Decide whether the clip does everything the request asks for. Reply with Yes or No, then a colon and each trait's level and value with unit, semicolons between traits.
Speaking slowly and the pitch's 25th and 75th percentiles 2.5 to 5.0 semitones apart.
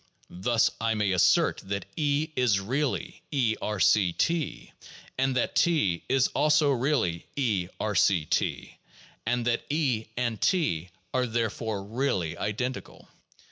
No: slow, 130 wpm; wide, 5.4 semitones